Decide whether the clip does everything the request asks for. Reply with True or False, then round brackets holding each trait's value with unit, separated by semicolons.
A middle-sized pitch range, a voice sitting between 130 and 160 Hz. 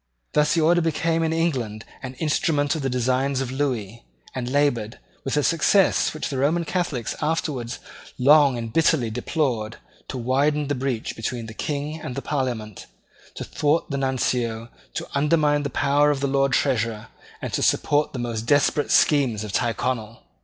True (3.7 semitones; 135 Hz)